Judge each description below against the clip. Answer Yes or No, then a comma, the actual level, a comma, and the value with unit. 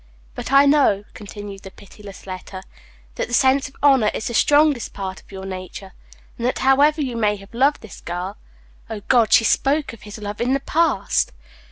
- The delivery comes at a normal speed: Yes, average, 195 wpm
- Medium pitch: No, high, 225 Hz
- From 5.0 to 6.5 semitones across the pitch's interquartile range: Yes, wide, 5.6 semitones